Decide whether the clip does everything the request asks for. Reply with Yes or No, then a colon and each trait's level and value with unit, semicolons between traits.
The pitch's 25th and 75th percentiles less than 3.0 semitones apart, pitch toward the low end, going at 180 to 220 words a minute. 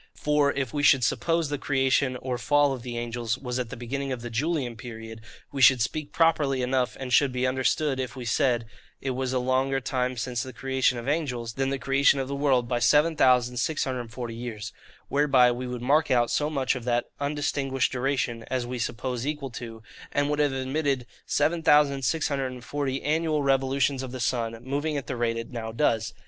Yes: narrow, 2.5 semitones; low, 130 Hz; average, 190 wpm